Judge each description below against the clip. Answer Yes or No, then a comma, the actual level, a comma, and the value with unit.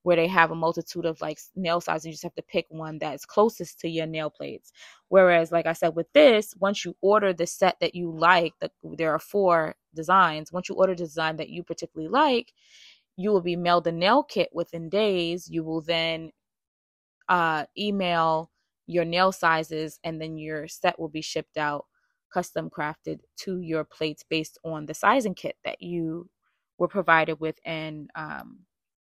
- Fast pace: No, average, 190 wpm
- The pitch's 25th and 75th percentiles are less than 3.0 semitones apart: Yes, narrow, 2.5 semitones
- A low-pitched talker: No, medium, 170 Hz